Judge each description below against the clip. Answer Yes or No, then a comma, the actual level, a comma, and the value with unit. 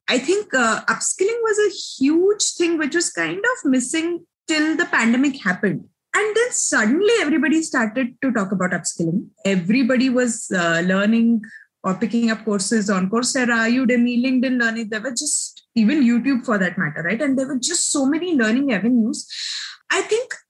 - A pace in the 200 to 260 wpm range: No, average, 170 wpm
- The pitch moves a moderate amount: No, wide, 7.0 semitones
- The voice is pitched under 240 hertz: No, very high, 260 Hz